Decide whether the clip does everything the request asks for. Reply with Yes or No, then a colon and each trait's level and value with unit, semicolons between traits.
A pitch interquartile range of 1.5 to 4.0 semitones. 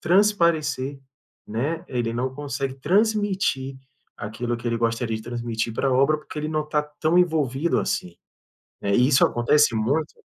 No: average, 4.6 semitones